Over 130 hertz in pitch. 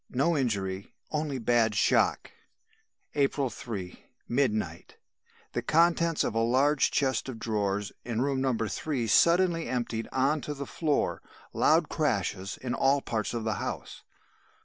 No: low, 125 Hz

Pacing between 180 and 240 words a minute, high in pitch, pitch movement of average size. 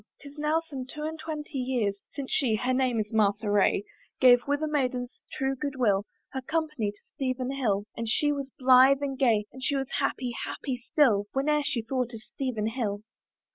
Yes: average, 195 wpm; very high, 260 Hz; average, 3.8 semitones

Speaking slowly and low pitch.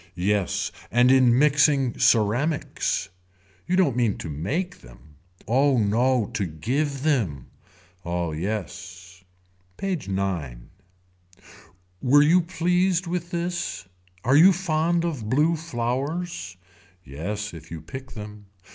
Yes: slow, 115 wpm; low, 120 Hz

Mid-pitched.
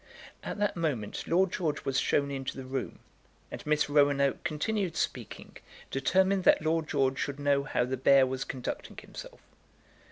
Yes: medium, 145 Hz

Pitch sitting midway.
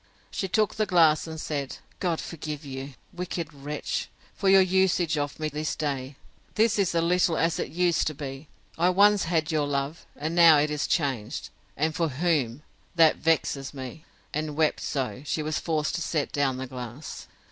Yes: medium, 155 Hz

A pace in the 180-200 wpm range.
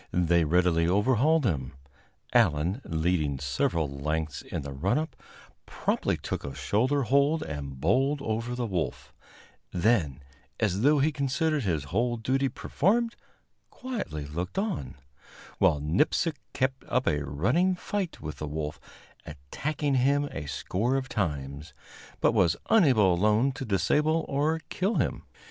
No: average, 140 wpm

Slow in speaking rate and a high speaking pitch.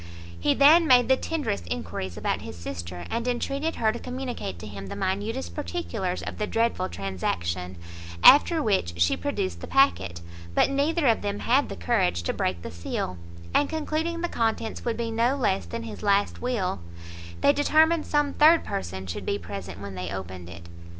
No: average, 185 wpm; high, 205 Hz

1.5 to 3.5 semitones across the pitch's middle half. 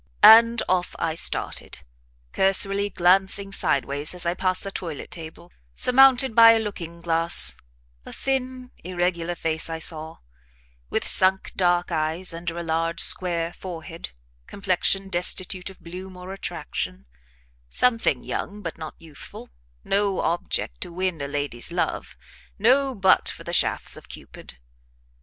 Yes: average, 2.9 semitones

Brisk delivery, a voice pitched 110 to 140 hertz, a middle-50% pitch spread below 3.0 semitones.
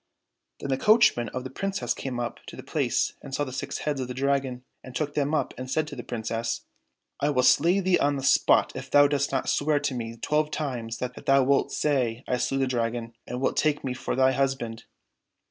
Yes: fast, 230 wpm; low, 135 Hz; narrow, 2.6 semitones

